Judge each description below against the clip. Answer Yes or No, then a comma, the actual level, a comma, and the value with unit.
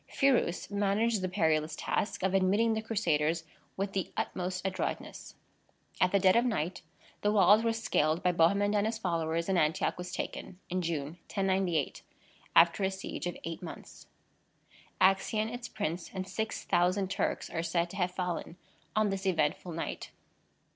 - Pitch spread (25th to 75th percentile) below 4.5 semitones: Yes, average, 3.1 semitones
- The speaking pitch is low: No, medium, 185 Hz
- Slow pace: No, average, 160 wpm